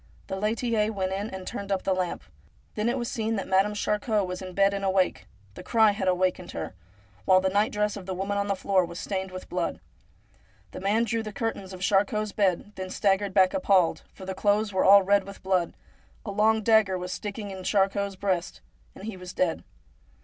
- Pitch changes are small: Yes, narrow, 2.0 semitones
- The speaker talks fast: Yes, fast, 220 wpm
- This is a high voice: Yes, high, 195 Hz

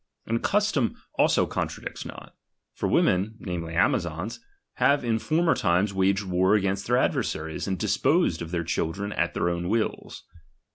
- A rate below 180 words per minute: Yes, average, 150 wpm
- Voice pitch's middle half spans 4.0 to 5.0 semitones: Yes, average, 4.5 semitones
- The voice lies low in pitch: Yes, very low, 95 Hz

